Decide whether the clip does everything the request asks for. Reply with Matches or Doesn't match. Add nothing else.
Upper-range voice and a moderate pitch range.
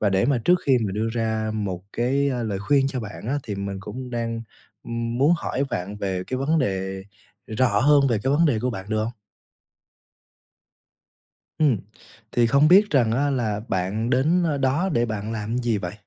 Doesn't match